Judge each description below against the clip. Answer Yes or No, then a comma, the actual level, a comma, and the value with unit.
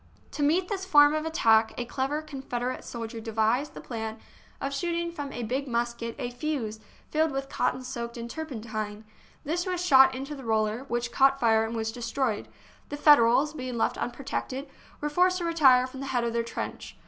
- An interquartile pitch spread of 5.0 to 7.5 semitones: No, average, 4.1 semitones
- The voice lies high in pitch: Yes, very high, 260 Hz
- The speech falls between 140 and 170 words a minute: No, average, 195 wpm